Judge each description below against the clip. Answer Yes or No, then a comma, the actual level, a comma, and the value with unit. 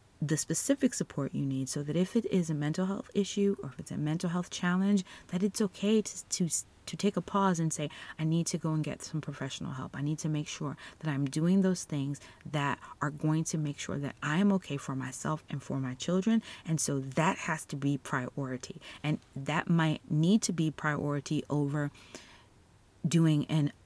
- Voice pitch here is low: No, medium, 155 Hz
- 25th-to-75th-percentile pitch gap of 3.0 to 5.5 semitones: Yes, average, 4.1 semitones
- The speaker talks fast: Yes, fast, 210 wpm